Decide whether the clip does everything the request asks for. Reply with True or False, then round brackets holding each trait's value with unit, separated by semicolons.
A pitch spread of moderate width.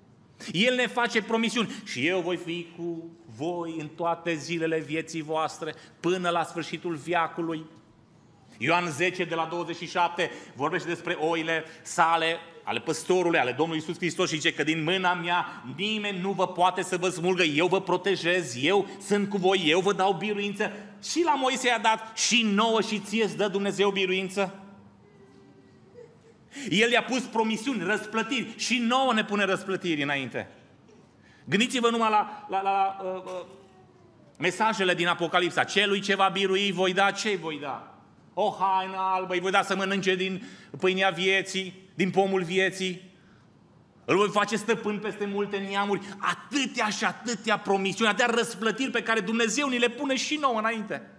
True (3.6 semitones)